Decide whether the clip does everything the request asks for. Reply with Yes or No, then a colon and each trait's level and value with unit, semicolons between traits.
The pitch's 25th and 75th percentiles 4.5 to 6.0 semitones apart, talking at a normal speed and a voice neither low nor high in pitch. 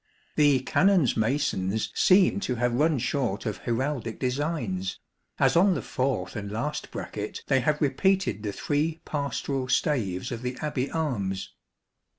No: average, 5.0 semitones; average, 145 wpm; low, 130 Hz